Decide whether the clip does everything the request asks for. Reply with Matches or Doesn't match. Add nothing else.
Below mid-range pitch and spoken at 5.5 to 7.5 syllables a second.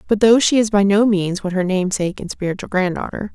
Doesn't match